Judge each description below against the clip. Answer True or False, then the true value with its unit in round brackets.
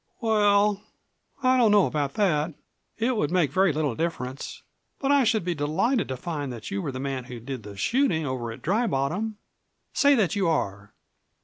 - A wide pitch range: True (7.9 semitones)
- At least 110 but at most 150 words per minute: False (190 wpm)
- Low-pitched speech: False (165 Hz)